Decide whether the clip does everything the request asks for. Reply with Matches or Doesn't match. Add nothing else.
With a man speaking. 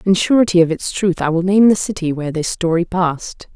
Doesn't match